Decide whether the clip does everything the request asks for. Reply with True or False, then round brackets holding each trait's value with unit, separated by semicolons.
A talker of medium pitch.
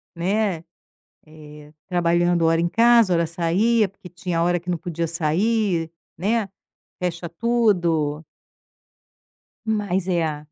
True (175 Hz)